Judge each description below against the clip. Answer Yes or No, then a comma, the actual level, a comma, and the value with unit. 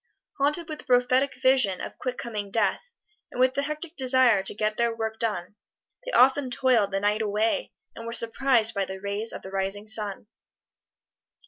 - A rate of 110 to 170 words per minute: No, average, 185 wpm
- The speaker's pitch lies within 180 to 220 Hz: No, high, 230 Hz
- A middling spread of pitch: Yes, average, 4.0 semitones